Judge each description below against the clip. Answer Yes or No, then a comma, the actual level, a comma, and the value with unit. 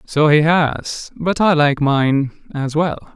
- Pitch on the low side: No, medium, 150 Hz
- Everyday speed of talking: Yes, average, 170 wpm